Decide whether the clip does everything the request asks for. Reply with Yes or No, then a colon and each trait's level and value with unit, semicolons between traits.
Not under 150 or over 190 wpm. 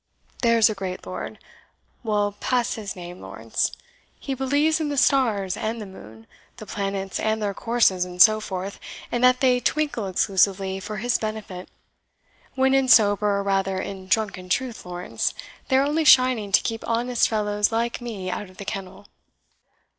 Yes: average, 170 wpm